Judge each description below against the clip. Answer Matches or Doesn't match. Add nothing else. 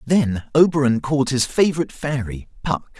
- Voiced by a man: Matches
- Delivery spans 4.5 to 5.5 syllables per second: Matches